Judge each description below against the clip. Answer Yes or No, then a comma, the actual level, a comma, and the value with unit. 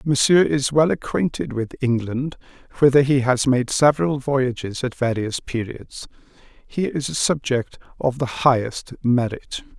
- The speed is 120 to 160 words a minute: Yes, average, 140 wpm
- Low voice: Yes, low, 130 Hz